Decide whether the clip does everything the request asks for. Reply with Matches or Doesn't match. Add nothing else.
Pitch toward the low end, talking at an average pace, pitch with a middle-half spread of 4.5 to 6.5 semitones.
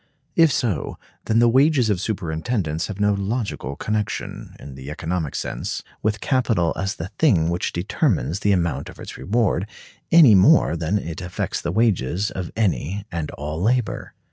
Matches